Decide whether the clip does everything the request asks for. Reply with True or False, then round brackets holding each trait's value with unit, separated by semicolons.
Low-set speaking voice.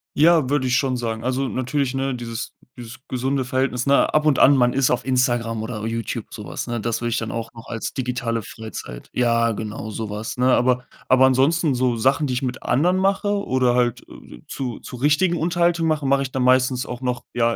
True (125 Hz)